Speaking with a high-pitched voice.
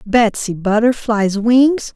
Yes: high, 225 Hz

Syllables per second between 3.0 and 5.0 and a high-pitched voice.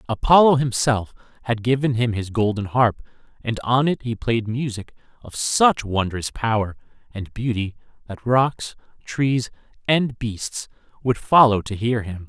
No: 4.3 syllables/s; low, 115 Hz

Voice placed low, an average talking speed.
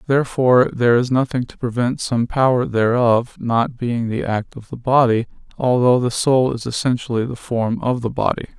Yes: low, 120 Hz; average, 180 wpm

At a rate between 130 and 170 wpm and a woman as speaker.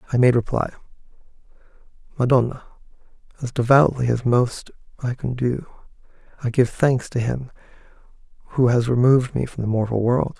No: average, 140 wpm; male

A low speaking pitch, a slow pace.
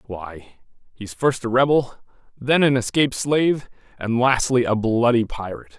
No: low, 120 Hz; average, 145 wpm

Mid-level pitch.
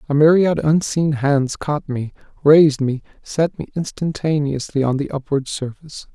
Yes: medium, 145 Hz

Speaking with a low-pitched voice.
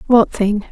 No: high, 215 Hz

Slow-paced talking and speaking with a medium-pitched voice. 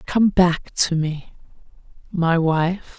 Yes: slow, 100 wpm; medium, 170 Hz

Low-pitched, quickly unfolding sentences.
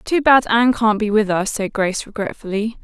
No: high, 215 Hz; fast, 210 wpm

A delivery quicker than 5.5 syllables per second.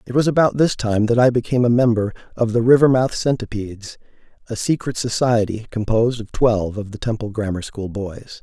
Yes: 5.7 syllables/s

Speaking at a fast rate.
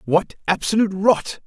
No: slow, 125 wpm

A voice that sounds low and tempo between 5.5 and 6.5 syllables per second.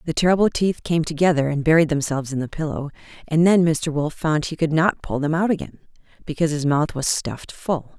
No: medium, 155 Hz; 5.9 syllables/s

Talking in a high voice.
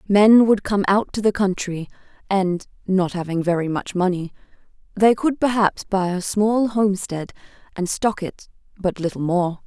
Yes: high, 195 Hz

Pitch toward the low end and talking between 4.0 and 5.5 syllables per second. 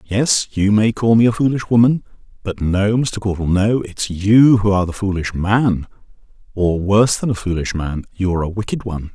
Yes: low, 100 Hz; 5.2 syllables/s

